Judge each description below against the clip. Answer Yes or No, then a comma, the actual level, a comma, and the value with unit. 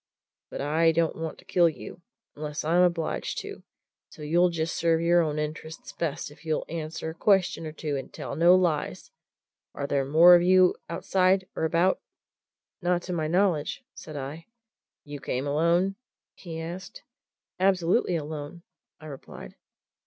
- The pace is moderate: Yes, average, 160 wpm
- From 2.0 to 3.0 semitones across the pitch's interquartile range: Yes, narrow, 2.5 semitones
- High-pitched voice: No, medium, 165 Hz